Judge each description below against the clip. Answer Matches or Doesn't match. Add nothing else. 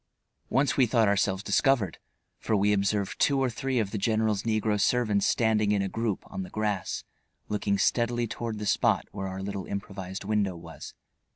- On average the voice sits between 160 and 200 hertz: Doesn't match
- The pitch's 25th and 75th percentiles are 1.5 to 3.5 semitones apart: Matches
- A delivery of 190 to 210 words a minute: Doesn't match